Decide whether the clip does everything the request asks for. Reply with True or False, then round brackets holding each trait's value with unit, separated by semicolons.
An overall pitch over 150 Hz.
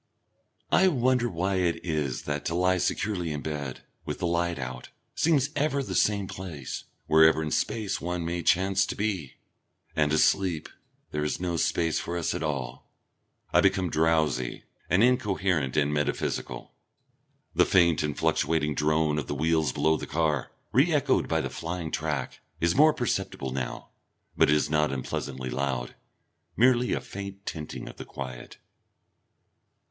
False (80 Hz)